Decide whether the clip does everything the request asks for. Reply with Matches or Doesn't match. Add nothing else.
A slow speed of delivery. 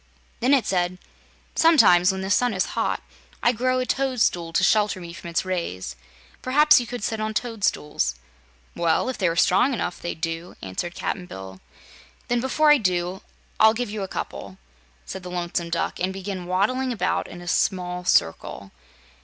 Doesn't match